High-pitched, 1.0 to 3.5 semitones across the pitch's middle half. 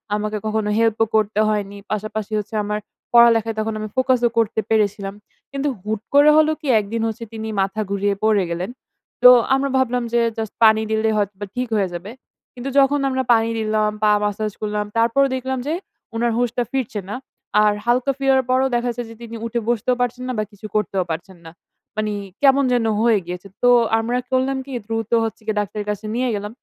Yes: high, 220 Hz; average, 2.9 semitones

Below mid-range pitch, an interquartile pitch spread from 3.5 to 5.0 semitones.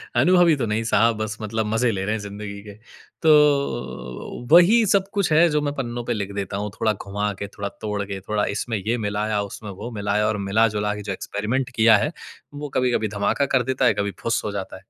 Yes: low, 110 Hz; average, 3.9 semitones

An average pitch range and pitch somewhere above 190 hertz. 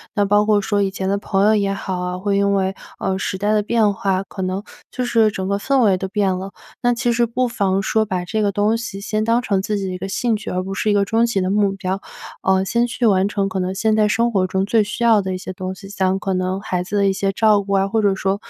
No: narrow, 2.1 semitones; high, 200 Hz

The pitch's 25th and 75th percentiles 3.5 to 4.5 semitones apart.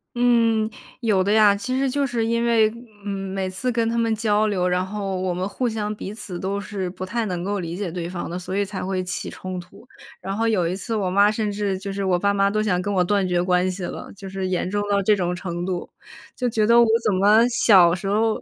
No: average, 2.8 semitones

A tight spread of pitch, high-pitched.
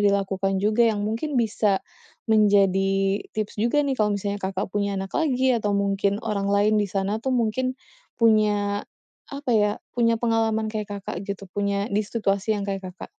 Yes: narrow, 2.0 semitones; high, 205 Hz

